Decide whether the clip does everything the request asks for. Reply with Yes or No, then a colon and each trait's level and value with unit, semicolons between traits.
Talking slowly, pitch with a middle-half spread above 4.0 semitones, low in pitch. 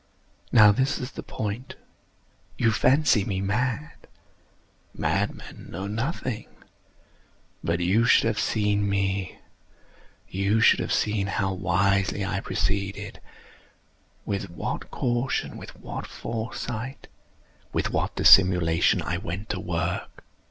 No: slow, 105 wpm; average, 2.9 semitones; low, 100 Hz